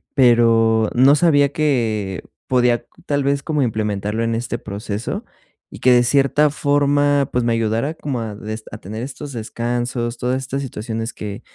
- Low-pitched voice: Yes, low, 120 Hz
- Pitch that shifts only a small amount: No, average, 3.8 semitones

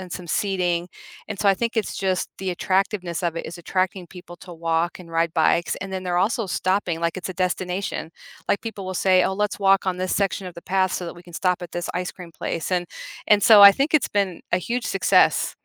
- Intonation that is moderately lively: No, narrow, 1.9 semitones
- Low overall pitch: No, medium, 185 Hz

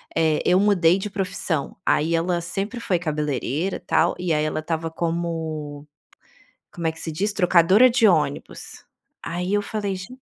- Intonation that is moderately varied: Yes, average, 3.3 semitones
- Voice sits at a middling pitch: Yes, medium, 170 Hz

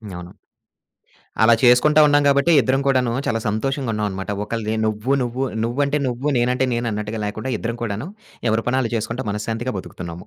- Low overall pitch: Yes, low, 115 Hz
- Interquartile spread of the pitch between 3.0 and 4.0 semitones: Yes, average, 3.6 semitones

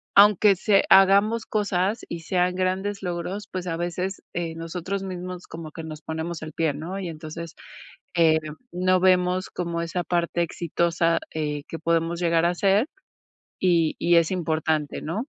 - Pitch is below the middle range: No, medium, 175 Hz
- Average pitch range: No, narrow, 2.1 semitones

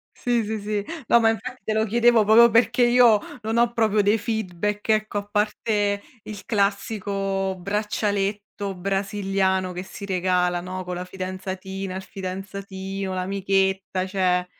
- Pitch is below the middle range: No, high, 200 Hz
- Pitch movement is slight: Yes, narrow, 2.2 semitones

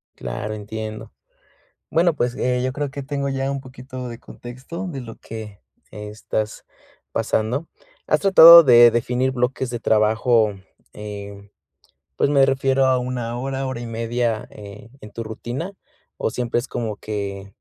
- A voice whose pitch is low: Yes, low, 120 Hz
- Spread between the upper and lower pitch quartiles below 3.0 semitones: No, average, 3.6 semitones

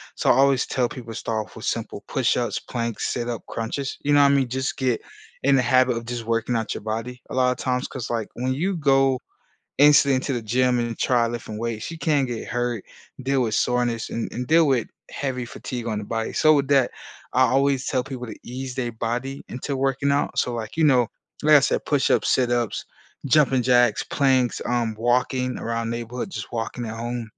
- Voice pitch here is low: Yes, low, 125 Hz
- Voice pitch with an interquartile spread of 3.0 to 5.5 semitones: No, narrow, 2.4 semitones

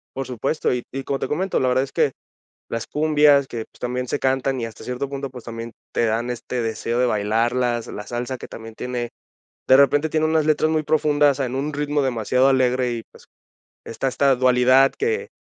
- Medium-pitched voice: No, low, 130 Hz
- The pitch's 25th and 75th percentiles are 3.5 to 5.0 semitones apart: No, average, 2.9 semitones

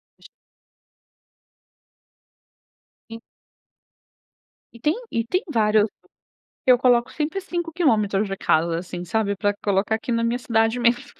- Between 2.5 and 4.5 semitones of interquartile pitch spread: Yes, average, 3.3 semitones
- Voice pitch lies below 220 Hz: No, high, 225 Hz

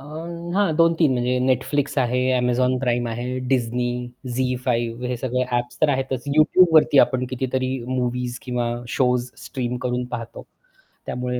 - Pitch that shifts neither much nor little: No, narrow, 1.3 semitones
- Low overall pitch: Yes, low, 125 Hz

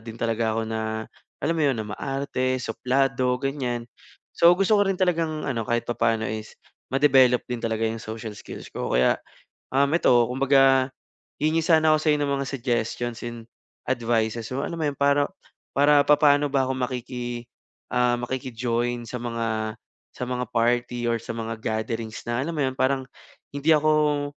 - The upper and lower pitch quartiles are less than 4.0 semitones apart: Yes, average, 3.5 semitones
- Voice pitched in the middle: No, low, 125 Hz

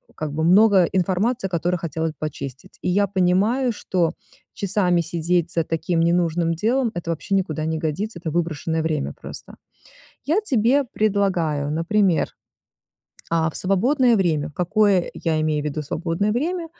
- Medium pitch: Yes, medium, 175 Hz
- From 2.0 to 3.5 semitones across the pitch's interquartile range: No, average, 4.1 semitones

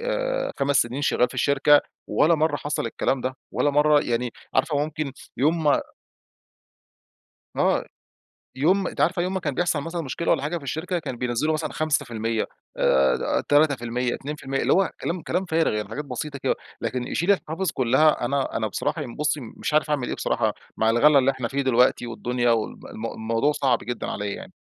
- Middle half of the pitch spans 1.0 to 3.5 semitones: No, average, 4.2 semitones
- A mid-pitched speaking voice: Yes, medium, 145 Hz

